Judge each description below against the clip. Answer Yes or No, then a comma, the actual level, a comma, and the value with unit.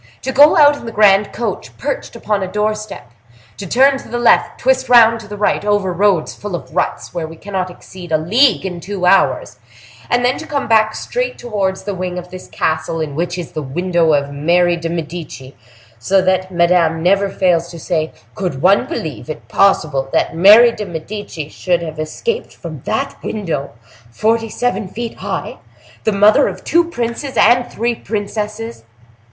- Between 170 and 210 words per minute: Yes, average, 180 wpm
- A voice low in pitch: No, high, 195 Hz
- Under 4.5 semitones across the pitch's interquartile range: No, average, 5.1 semitones